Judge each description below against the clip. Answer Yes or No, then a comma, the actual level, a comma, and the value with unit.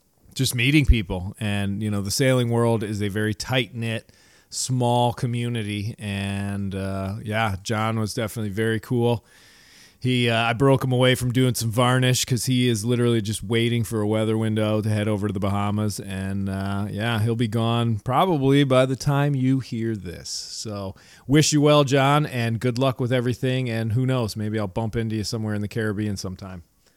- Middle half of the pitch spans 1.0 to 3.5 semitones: Yes, average, 3.2 semitones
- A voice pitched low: Yes, low, 115 Hz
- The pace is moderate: Yes, average, 190 wpm